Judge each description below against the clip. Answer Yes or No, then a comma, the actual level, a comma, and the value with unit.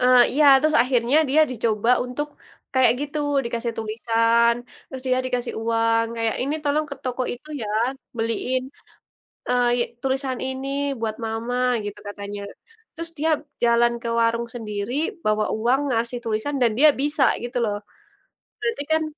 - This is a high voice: Yes, high, 240 Hz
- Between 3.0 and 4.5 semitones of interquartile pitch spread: No, narrow, 2.5 semitones